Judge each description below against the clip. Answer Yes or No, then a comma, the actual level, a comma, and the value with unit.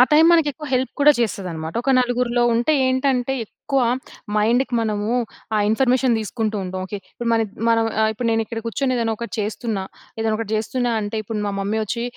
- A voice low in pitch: No, high, 230 Hz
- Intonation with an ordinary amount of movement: Yes, average, 3.0 semitones